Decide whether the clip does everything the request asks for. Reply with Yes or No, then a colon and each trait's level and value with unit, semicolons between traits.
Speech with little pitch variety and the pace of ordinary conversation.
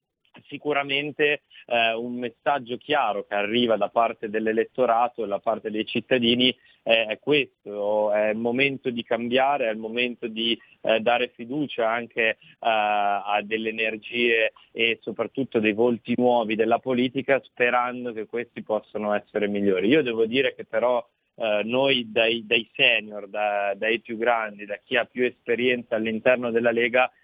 Yes: narrow, 2.1 semitones; average, 150 wpm